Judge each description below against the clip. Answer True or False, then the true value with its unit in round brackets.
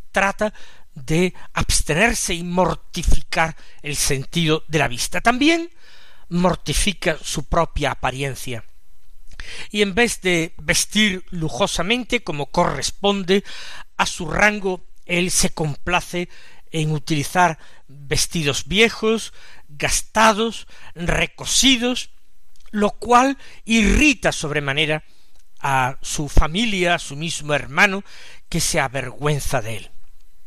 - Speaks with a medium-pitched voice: True (170 Hz)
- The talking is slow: True (100 wpm)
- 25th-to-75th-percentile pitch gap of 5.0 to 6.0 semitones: True (5.6 semitones)